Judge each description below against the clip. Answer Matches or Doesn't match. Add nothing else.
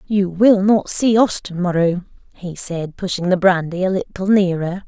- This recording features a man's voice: Doesn't match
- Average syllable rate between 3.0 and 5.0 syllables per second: Matches